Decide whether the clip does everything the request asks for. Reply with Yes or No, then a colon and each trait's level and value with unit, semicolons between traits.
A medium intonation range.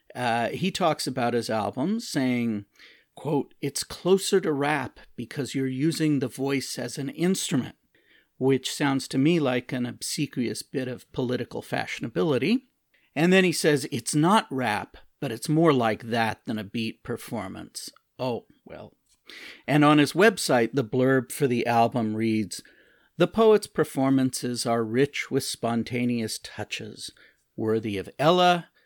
Yes: average, 4.6 semitones